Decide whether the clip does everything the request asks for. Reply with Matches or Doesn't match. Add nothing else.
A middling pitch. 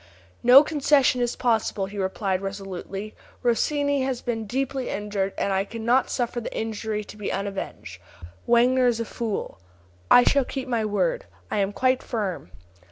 Doesn't match